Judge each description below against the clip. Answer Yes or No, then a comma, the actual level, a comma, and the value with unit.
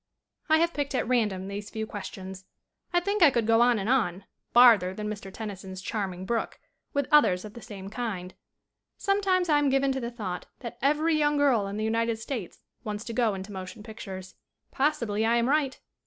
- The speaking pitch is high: Yes, high, 225 Hz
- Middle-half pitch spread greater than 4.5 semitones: Yes, wide, 5.4 semitones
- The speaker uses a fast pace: Yes, fast, 210 wpm